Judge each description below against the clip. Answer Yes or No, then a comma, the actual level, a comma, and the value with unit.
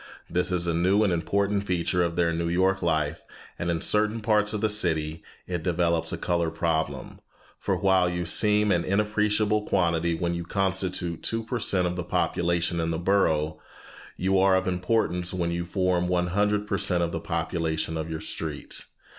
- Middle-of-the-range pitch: No, very low, 90 Hz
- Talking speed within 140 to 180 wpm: No, average, 190 wpm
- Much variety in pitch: No, average, 2.7 semitones